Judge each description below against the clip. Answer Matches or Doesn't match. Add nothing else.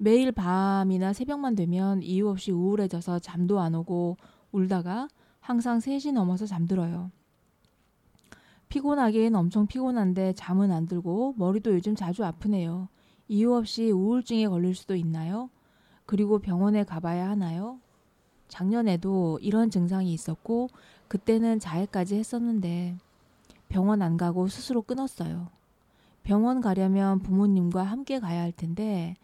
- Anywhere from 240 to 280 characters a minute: Doesn't match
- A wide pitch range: Doesn't match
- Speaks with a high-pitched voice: Matches